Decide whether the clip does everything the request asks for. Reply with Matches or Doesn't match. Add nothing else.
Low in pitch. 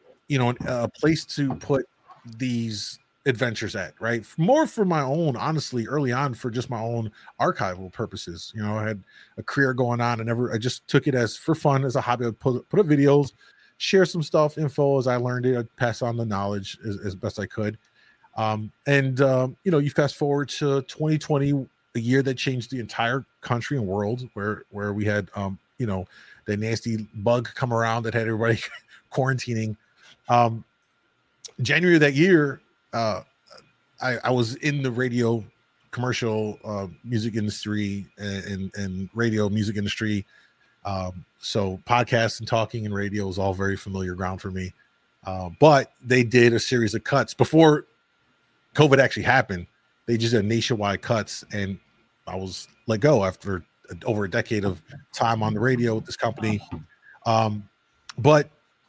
Matches